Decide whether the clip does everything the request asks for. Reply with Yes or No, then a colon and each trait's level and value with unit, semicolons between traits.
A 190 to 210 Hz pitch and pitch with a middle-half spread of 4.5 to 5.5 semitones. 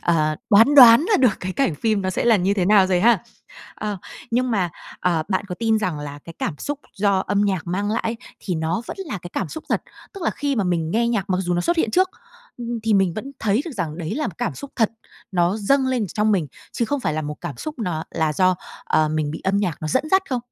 Yes: high, 200 Hz; average, 5.1 semitones